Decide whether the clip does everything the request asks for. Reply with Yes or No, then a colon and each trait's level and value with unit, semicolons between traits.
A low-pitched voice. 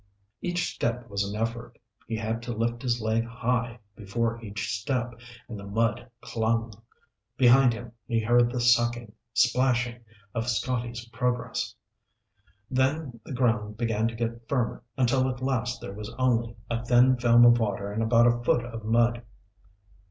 Yes: low, 120 Hz